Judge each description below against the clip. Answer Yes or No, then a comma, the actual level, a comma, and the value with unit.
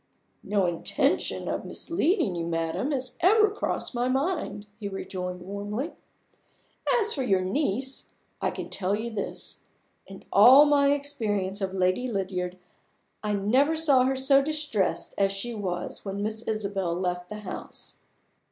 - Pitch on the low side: No, high, 210 Hz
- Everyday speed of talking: Yes, average, 145 wpm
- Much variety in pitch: Yes, wide, 6.2 semitones